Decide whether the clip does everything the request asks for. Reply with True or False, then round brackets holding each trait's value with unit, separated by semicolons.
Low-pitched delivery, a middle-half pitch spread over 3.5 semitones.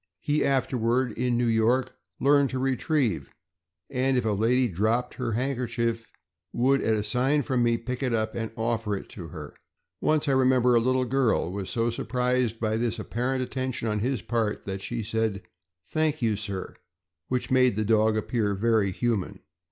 False (120 Hz; 2.8 semitones)